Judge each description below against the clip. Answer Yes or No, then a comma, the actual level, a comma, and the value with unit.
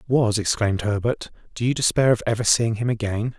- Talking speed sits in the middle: Yes, average, 195 wpm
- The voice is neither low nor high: No, low, 115 Hz